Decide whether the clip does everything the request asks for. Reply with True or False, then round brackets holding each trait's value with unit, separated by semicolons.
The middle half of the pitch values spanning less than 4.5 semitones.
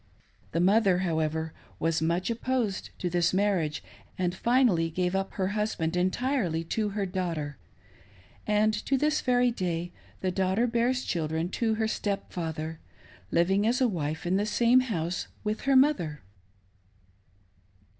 False (5.2 semitones)